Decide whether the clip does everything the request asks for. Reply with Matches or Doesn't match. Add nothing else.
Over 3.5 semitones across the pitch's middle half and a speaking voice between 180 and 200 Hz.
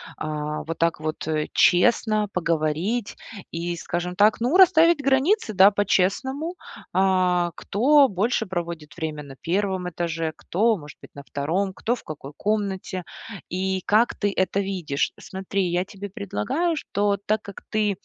Matches